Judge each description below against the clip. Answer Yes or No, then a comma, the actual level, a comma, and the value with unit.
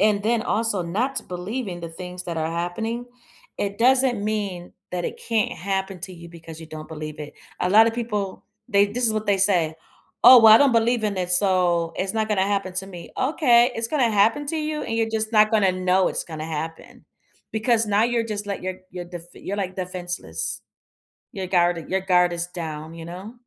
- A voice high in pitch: Yes, high, 195 Hz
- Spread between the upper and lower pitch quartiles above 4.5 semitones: No, average, 4.1 semitones